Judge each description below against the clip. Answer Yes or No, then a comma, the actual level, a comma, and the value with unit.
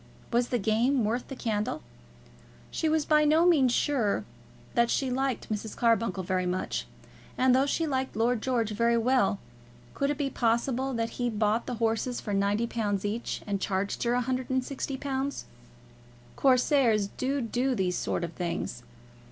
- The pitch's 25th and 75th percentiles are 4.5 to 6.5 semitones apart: No, average, 3.7 semitones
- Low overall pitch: No, high, 240 Hz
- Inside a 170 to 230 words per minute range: No, average, 155 wpm